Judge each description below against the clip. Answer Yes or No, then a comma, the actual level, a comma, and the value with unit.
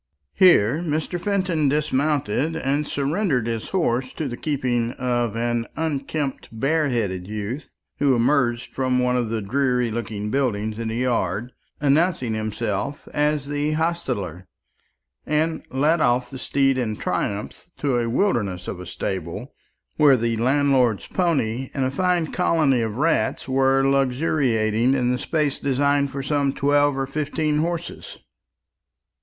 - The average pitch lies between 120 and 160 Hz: Yes, low, 135 Hz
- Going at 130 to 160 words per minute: Yes, average, 140 wpm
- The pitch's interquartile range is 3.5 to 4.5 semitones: Yes, average, 4.2 semitones